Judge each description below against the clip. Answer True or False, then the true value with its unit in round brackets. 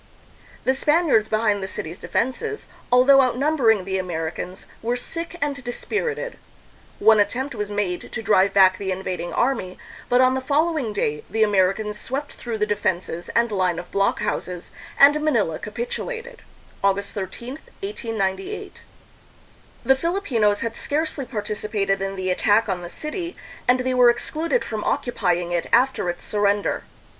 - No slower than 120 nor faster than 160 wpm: True (145 wpm)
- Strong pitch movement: True (5.9 semitones)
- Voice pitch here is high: True (220 Hz)